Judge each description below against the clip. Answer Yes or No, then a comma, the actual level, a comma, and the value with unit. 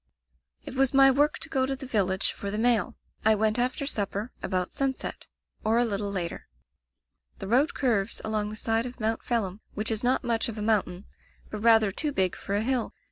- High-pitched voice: Yes, high, 225 Hz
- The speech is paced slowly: No, fast, 205 wpm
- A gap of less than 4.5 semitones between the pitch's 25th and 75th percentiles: Yes, average, 3.6 semitones